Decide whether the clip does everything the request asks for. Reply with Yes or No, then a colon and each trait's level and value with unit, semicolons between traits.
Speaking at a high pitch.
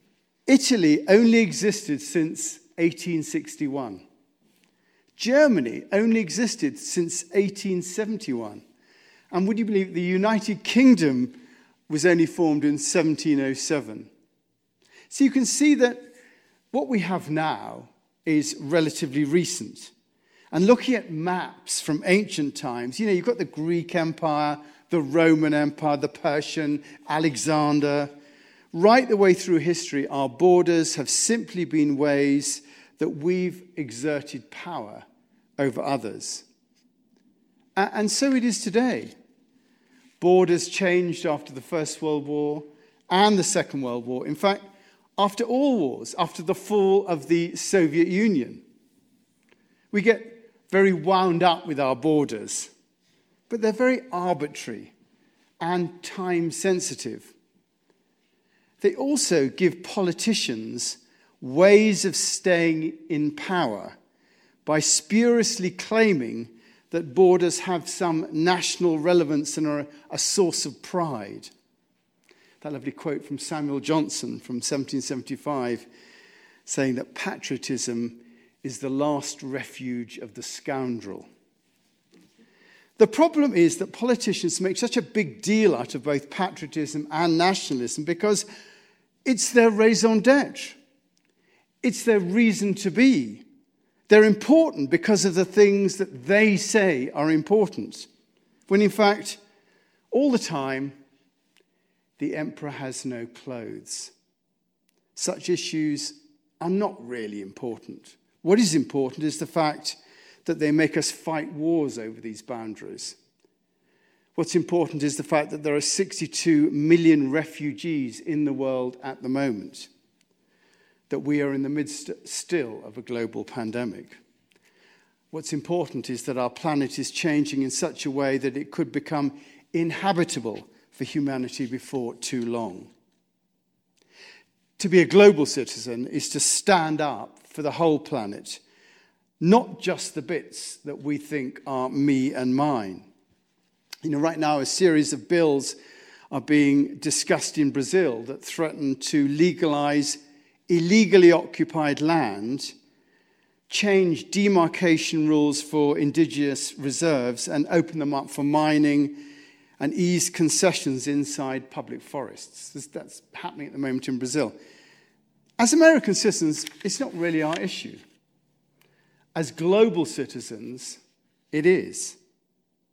No: medium, 165 Hz